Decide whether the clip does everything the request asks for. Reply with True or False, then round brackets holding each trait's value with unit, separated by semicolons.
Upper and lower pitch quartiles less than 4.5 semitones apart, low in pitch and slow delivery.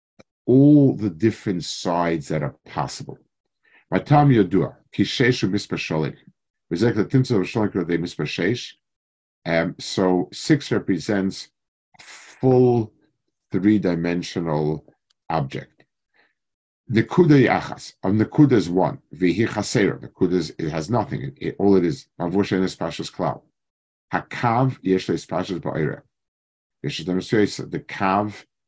False (5.1 semitones; 100 Hz; 120 wpm)